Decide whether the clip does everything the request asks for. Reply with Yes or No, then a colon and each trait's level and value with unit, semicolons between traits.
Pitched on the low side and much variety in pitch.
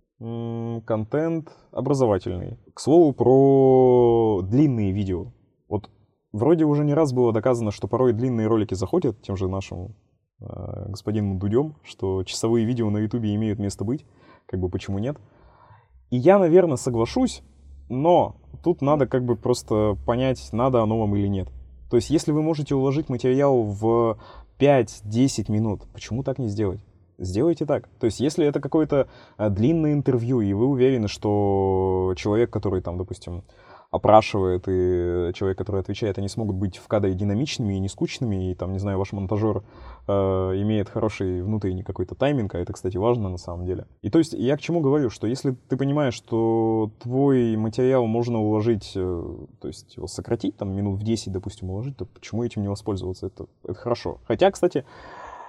No: low, 110 Hz; average, 4.8 semitones